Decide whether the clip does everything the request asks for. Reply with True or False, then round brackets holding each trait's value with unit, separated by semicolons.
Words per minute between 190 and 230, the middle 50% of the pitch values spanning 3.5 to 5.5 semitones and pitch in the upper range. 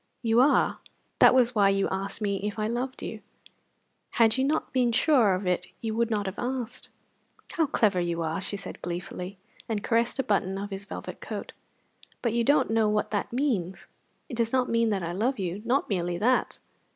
True (200 wpm; 3.8 semitones; 215 Hz)